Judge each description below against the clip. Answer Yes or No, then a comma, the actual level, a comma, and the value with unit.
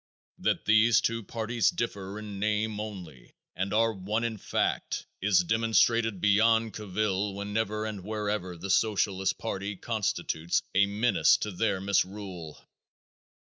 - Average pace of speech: No, slow, 130 wpm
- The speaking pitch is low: Yes, low, 105 Hz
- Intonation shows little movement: Yes, narrow, 2.3 semitones